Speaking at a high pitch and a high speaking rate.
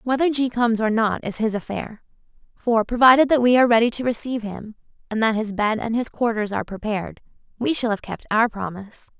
Yes: high, 225 Hz; fast, 210 wpm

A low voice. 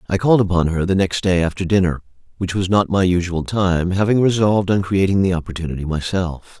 Yes: very low, 95 Hz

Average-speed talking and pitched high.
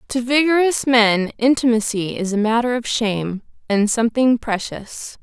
No: slow, 125 wpm; high, 230 Hz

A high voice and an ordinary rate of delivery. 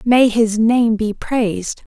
Yes: high, 225 Hz; average, 155 wpm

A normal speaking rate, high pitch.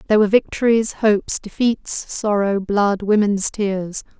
No: slow, 130 wpm; high, 205 Hz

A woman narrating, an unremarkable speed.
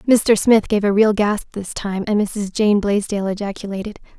Yes: female; average, 185 wpm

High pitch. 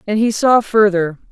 Yes: high, 210 Hz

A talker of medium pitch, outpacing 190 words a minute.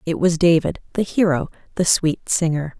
No: medium, 165 Hz; average, 170 wpm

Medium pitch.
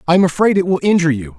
Yes: medium, 165 Hz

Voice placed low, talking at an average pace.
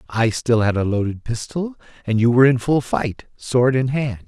No: low, 125 Hz; fast, 210 wpm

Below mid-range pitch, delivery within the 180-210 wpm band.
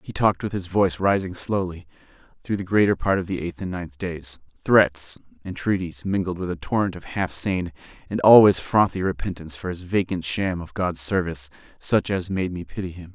Yes: very low, 90 Hz; average, 190 wpm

